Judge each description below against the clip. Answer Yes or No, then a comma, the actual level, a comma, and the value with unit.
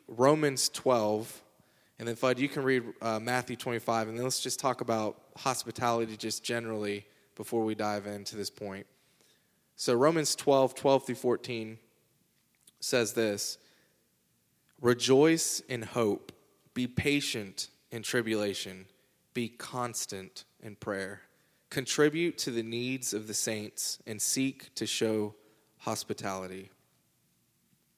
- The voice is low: Yes, low, 115 Hz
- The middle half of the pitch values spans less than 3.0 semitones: No, average, 3.4 semitones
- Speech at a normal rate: No, slow, 120 wpm